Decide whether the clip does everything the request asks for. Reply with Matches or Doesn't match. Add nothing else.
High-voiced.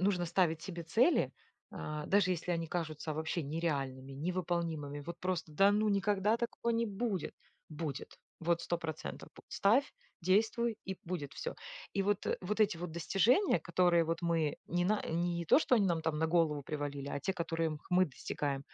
Doesn't match